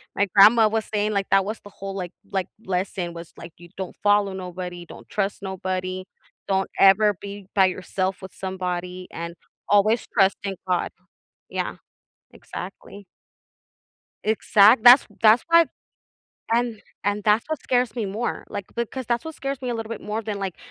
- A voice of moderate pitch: No, high, 200 Hz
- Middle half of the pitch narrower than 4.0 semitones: Yes, average, 2.8 semitones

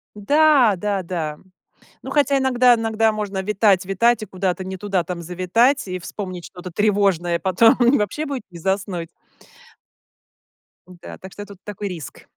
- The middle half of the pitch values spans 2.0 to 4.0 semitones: Yes, average, 3.7 semitones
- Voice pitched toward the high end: Yes, high, 195 Hz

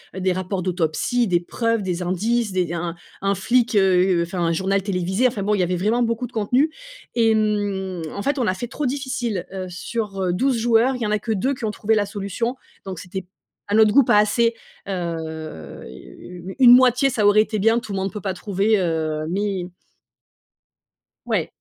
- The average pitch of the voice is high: Yes, high, 200 Hz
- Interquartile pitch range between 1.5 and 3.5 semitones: No, average, 4.0 semitones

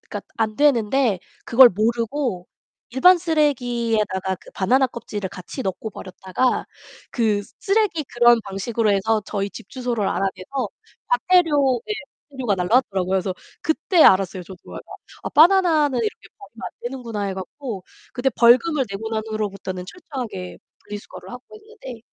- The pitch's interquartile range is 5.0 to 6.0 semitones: Yes, wide, 5.5 semitones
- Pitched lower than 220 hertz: No, high, 235 Hz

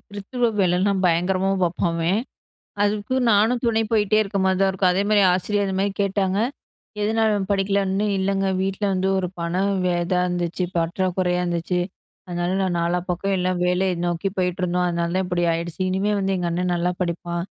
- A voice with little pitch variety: Yes, narrow, 2.0 semitones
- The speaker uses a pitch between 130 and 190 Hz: Yes, medium, 185 Hz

